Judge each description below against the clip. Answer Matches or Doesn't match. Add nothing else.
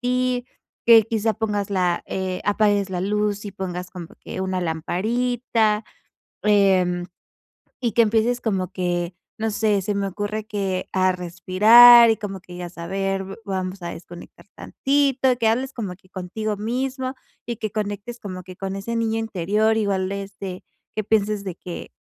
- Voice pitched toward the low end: Doesn't match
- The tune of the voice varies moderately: Matches